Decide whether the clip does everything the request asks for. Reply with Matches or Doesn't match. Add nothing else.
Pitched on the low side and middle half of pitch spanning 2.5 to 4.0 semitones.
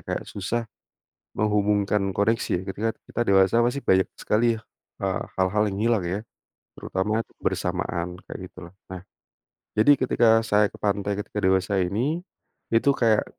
Matches